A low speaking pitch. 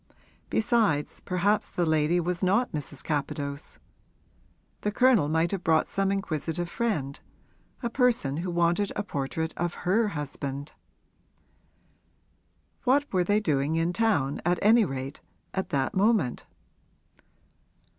No: medium, 175 Hz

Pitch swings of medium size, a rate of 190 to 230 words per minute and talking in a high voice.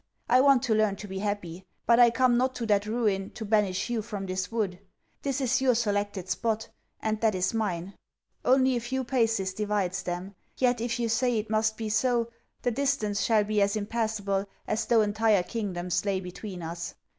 Yes: average, 3.2 semitones; average, 195 wpm; high, 215 Hz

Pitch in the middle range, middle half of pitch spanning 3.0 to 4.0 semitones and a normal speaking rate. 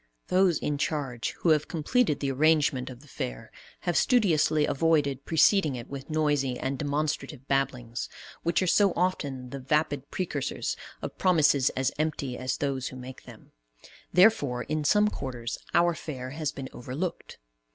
Yes: medium, 145 Hz; average, 3.5 semitones; average, 155 wpm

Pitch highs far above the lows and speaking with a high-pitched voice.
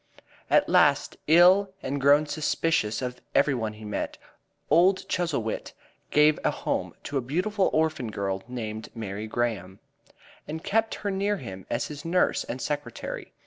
No: wide, 7.3 semitones; medium, 140 Hz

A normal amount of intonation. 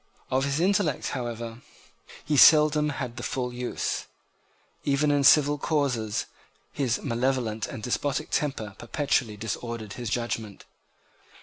Yes: average, 3.8 semitones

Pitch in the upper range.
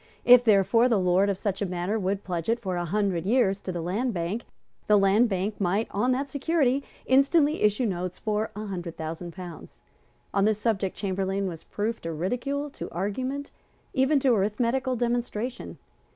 Yes: high, 210 Hz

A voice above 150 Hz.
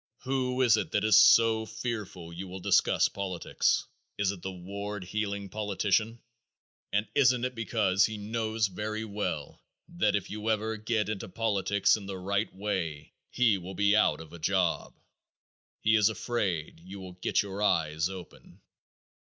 No: low, 105 Hz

